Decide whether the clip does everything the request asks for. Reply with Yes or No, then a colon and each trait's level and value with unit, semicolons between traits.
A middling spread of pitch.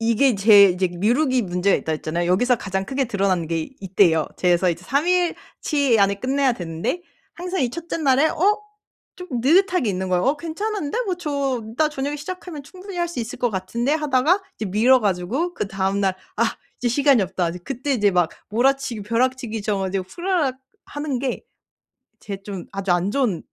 No: wide, 7.2 semitones